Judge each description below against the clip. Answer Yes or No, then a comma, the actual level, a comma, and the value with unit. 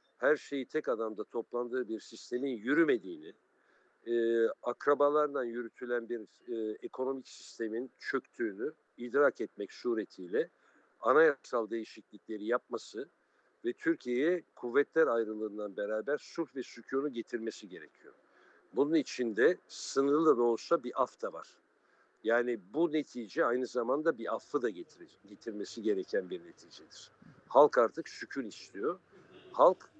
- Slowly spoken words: Yes, slow, 115 wpm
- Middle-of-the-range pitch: No, low, 130 Hz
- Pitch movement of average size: No, wide, 6.3 semitones